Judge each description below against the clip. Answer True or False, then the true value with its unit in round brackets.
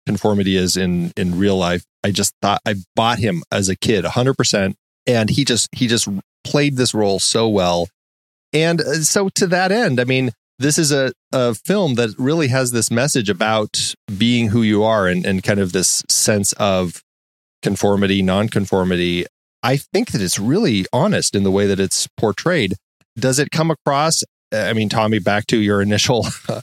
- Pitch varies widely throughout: False (4.7 semitones)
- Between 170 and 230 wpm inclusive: True (185 wpm)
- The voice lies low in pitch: True (105 Hz)